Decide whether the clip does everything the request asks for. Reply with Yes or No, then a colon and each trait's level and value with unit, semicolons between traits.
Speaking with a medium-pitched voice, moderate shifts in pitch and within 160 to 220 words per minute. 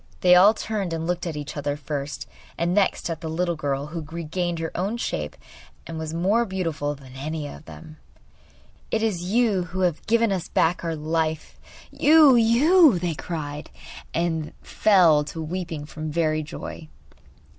Yes: medium, 165 Hz; average, 3.3 semitones; average, 170 wpm